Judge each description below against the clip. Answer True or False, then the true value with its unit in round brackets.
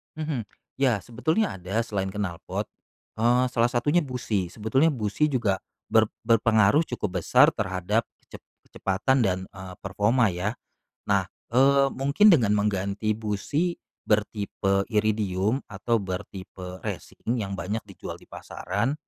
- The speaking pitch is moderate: False (110 Hz)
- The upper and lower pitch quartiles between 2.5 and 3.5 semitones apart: False (4.3 semitones)